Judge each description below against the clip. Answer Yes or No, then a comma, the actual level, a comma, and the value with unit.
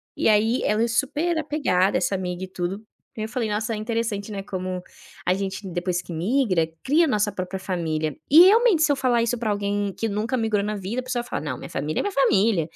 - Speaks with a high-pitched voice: Yes, high, 210 Hz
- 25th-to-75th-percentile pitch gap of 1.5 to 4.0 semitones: No, average, 4.6 semitones